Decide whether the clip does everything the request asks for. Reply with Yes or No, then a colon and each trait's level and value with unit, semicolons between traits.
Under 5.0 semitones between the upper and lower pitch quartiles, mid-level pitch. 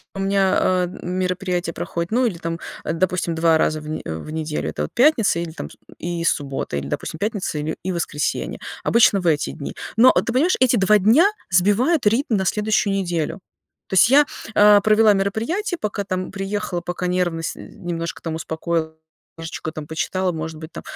Yes: average, 4.2 semitones; medium, 180 Hz